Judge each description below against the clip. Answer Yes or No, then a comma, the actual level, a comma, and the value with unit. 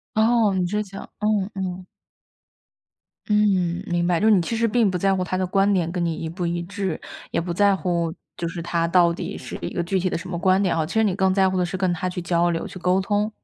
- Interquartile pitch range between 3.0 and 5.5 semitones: No, narrow, 2.4 semitones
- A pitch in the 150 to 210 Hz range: Yes, medium, 185 Hz